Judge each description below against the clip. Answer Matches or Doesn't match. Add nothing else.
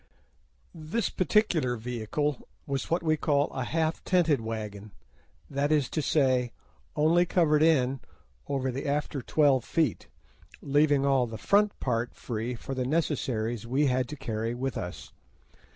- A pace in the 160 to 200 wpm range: Doesn't match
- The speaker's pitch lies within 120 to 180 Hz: Matches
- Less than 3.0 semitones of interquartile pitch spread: Doesn't match